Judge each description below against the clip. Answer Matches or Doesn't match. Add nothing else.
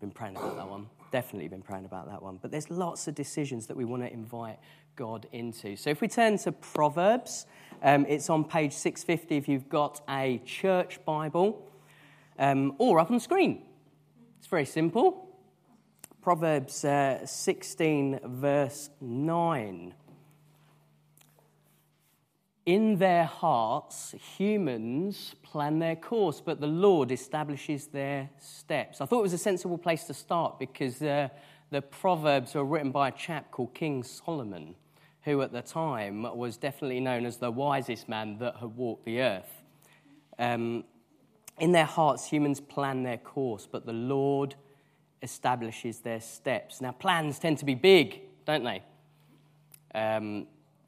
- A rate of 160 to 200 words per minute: Doesn't match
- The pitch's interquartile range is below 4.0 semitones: Doesn't match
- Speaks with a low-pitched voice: Doesn't match